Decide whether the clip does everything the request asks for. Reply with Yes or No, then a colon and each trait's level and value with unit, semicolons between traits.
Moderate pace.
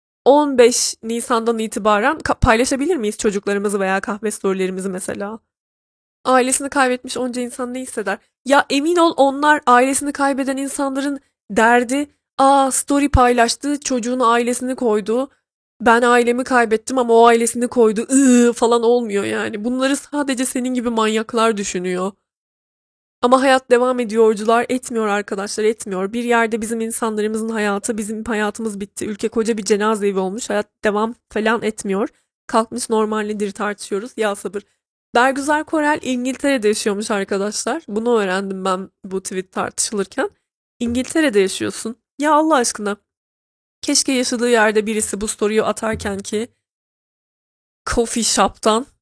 Yes: average, 125 wpm